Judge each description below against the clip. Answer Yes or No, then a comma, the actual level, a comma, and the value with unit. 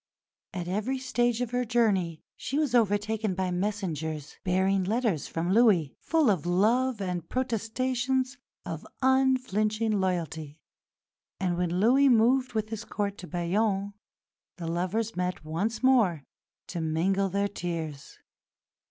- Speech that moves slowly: Yes, slow, 130 wpm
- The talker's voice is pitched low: No, high, 205 Hz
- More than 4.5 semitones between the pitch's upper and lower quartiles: Yes, average, 5.1 semitones